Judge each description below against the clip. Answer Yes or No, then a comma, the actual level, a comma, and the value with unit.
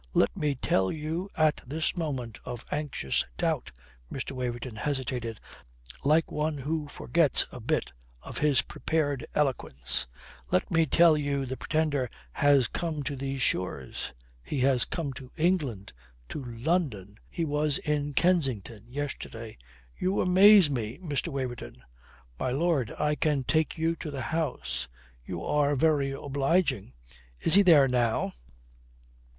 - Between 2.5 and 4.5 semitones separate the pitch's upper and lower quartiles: Yes, average, 4.2 semitones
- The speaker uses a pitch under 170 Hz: Yes, medium, 140 Hz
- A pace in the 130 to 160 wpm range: Yes, average, 140 wpm